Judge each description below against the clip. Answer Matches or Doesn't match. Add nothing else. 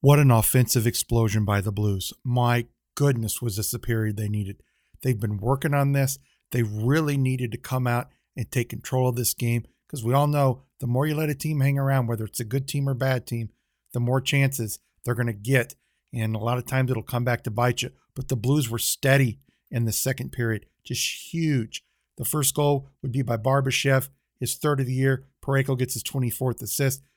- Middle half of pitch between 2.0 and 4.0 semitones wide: Matches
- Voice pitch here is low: Matches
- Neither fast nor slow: Doesn't match